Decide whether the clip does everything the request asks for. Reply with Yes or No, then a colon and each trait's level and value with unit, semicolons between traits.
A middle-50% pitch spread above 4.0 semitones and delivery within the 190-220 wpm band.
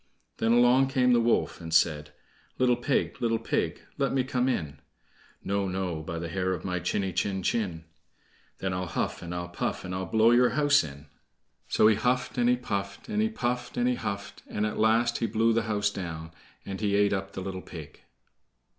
Yes: average, 5.1 semitones; fast, 205 wpm